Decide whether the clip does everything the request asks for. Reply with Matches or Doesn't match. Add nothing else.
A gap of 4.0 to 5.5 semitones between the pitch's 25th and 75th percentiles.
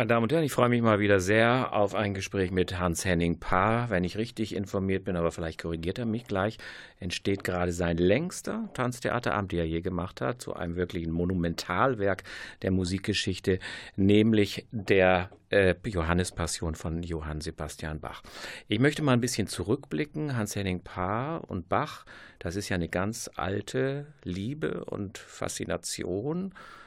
Matches